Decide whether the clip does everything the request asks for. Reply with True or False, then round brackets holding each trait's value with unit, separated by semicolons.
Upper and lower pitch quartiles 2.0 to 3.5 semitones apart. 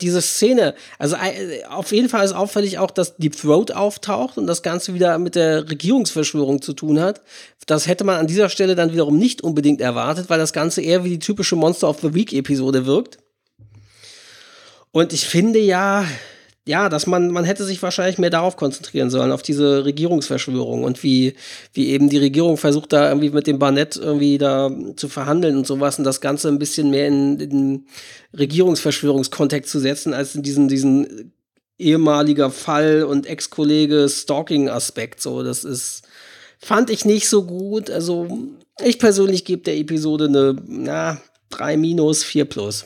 False (4.3 semitones)